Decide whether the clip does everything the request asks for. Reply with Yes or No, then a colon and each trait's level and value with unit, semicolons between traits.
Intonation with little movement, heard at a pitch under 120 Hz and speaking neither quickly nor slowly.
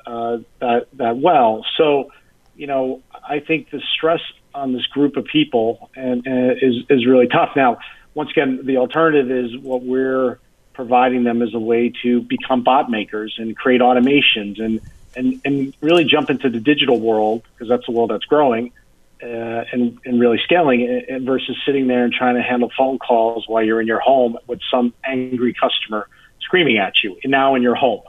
No: narrow, 2.3 semitones; low, 125 Hz; average, 190 wpm